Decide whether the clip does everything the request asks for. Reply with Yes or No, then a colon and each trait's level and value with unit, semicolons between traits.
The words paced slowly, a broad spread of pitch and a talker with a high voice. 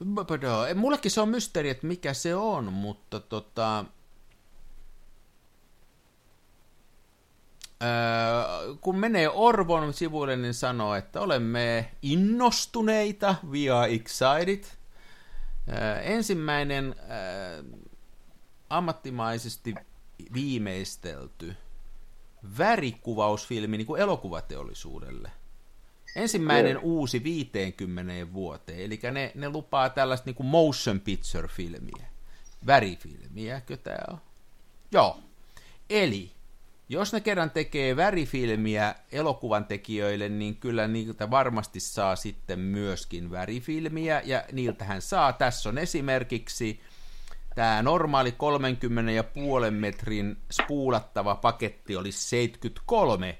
No: slow, 85 wpm; wide, 6.1 semitones; low, 120 Hz